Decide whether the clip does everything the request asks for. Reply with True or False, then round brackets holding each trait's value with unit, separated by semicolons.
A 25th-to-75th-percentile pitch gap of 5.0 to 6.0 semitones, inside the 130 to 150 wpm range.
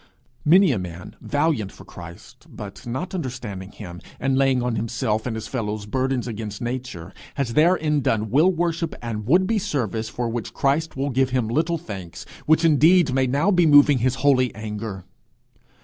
False (5.6 semitones; 175 wpm)